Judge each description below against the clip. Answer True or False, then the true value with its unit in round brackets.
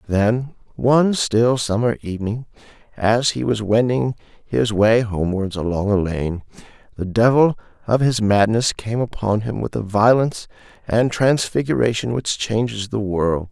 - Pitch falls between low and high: False (110 Hz)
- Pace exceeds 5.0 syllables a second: False (4.5 syllables/s)